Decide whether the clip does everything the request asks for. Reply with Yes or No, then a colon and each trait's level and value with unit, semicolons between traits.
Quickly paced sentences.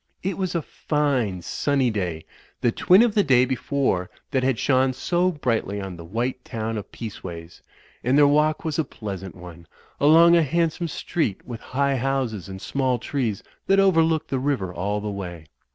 No: average, 180 wpm